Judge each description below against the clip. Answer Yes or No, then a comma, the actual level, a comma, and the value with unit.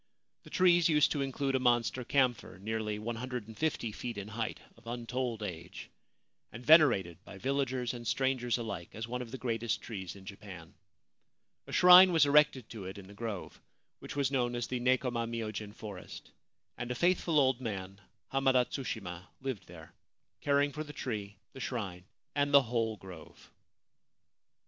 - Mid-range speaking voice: No, low, 120 Hz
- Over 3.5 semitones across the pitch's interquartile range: Yes, average, 4.3 semitones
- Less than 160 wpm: No, average, 165 wpm